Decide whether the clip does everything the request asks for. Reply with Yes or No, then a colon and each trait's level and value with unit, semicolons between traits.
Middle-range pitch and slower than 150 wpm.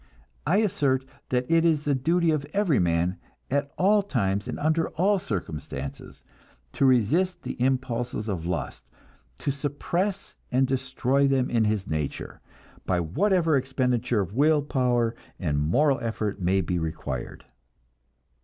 No: low, 130 Hz; average, 140 wpm